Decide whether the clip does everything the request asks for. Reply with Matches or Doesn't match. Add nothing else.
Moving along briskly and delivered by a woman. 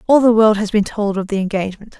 Matches